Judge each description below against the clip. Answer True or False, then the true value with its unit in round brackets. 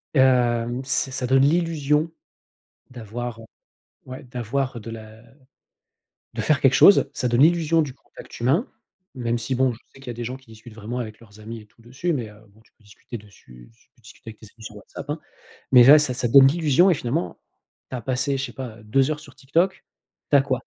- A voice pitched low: True (125 Hz)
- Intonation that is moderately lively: True (3.3 semitones)